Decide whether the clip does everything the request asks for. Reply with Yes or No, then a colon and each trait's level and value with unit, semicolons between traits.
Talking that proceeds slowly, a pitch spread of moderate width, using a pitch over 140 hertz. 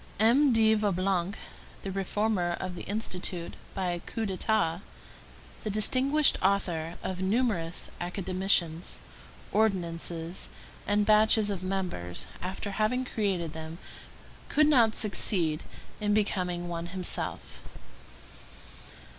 Yes: slow, 105 wpm; average, 3.6 semitones; high, 190 Hz